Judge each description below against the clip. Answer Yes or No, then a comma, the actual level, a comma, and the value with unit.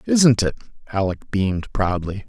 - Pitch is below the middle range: Yes, low, 105 Hz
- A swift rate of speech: No, slow, 130 wpm